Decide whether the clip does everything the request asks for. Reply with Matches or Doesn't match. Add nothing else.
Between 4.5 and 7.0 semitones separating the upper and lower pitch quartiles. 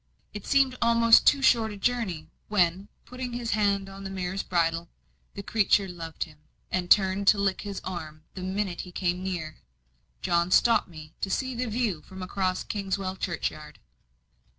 Doesn't match